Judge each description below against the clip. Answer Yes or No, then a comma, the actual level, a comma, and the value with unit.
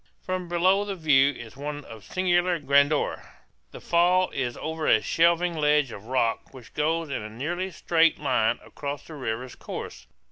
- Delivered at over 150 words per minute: Yes, average, 170 wpm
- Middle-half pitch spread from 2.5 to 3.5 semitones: No, average, 4.8 semitones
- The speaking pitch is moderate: Yes, medium, 150 Hz